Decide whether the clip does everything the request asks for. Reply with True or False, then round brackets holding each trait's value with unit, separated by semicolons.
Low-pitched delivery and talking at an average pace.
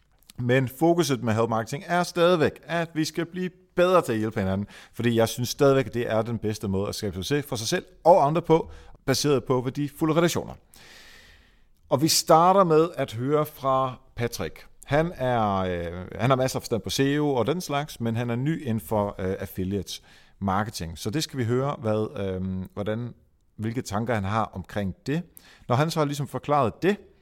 True (125 Hz; 200 wpm)